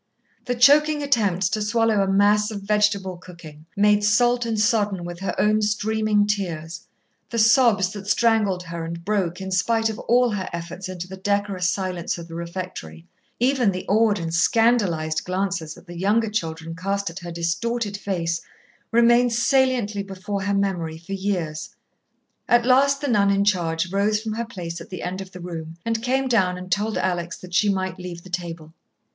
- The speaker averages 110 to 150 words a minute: No, average, 185 wpm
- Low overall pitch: No, high, 195 Hz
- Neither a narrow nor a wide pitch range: Yes, average, 3.9 semitones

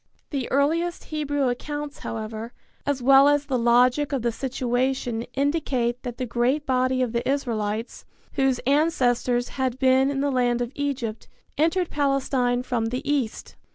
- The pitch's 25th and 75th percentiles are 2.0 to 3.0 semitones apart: Yes, average, 2.7 semitones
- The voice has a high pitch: Yes, very high, 260 Hz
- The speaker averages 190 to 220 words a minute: No, average, 155 wpm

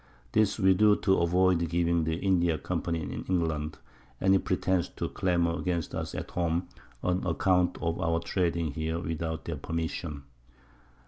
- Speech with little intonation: Yes, narrow, 2.0 semitones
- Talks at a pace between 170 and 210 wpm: No, average, 150 wpm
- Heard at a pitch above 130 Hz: No, very low, 85 Hz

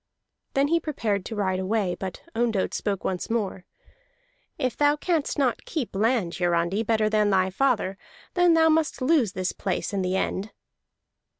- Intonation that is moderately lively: No, wide, 5.7 semitones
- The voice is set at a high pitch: Yes, high, 215 Hz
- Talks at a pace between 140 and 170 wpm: Yes, average, 165 wpm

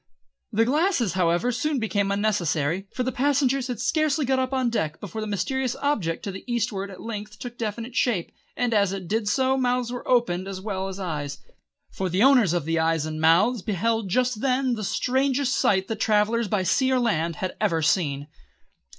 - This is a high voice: Yes, high, 215 Hz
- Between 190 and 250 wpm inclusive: Yes, average, 195 wpm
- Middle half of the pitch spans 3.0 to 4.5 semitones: No, average, 5.2 semitones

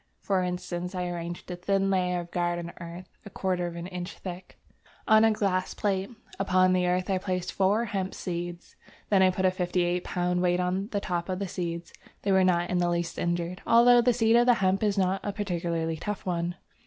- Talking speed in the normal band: No, fast, 215 wpm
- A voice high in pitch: No, medium, 180 Hz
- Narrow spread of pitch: Yes, narrow, 1.9 semitones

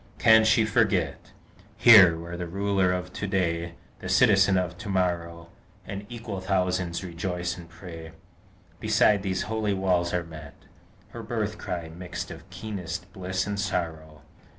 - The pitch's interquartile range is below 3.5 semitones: Yes, narrow, 2.5 semitones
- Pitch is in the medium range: No, very low, 90 Hz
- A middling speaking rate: Yes, average, 150 wpm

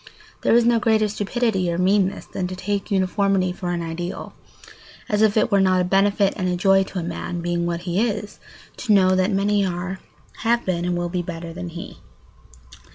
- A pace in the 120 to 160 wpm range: No, fast, 205 wpm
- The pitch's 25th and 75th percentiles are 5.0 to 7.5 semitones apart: No, narrow, 2.5 semitones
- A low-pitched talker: No, medium, 185 Hz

